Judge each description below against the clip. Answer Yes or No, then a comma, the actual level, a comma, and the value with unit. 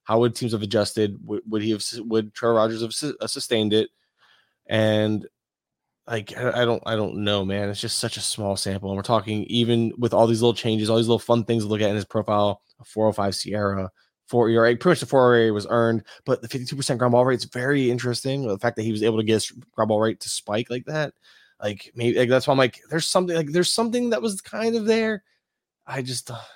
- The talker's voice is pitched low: Yes, low, 115 Hz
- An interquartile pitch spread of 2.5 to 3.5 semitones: Yes, average, 2.8 semitones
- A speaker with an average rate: No, fast, 245 wpm